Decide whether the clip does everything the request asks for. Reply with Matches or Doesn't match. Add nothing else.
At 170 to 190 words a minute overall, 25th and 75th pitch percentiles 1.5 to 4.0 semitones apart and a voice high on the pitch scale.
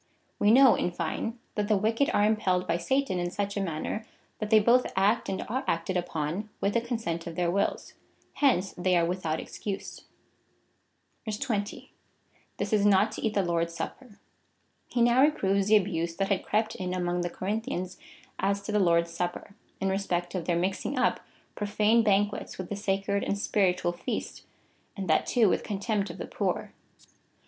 Matches